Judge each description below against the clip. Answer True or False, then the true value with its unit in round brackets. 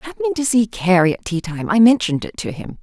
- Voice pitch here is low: False (205 Hz)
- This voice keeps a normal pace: False (235 wpm)